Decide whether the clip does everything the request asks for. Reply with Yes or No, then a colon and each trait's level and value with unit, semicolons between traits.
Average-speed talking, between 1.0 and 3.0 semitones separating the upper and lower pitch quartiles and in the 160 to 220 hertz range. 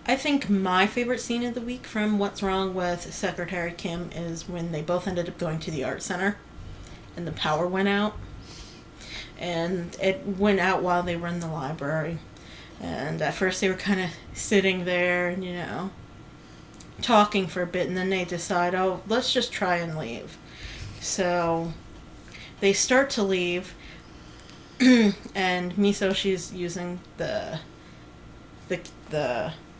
Yes: average, 155 wpm; narrow, 2.4 semitones; medium, 185 Hz